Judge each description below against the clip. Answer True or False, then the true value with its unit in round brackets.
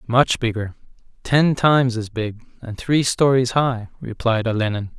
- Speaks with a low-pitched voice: True (120 Hz)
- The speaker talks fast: False (145 wpm)